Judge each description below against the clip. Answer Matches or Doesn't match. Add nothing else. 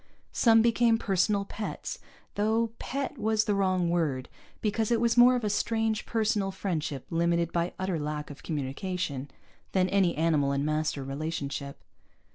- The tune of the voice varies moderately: Doesn't match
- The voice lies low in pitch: Doesn't match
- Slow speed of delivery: Doesn't match